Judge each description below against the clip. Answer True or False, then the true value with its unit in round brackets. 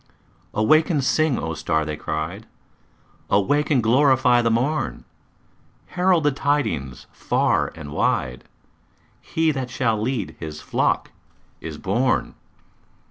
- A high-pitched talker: False (120 Hz)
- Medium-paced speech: False (120 wpm)